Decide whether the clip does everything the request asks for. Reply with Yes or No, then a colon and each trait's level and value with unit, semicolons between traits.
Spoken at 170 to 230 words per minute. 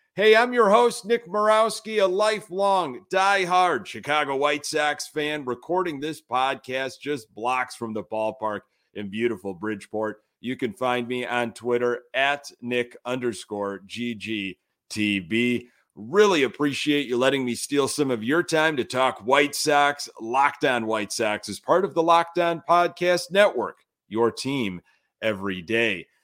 No: average, 140 wpm